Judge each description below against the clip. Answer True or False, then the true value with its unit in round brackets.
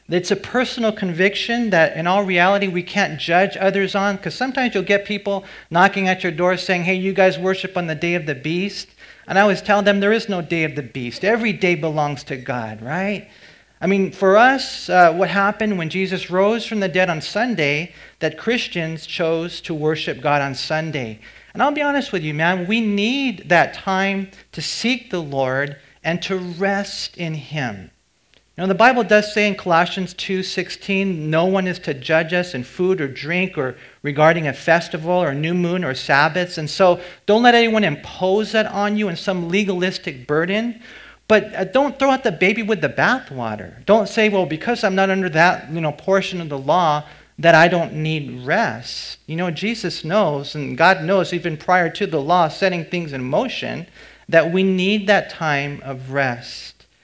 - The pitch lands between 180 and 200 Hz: True (185 Hz)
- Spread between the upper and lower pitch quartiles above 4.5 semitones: False (3.9 semitones)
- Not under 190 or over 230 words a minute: True (195 wpm)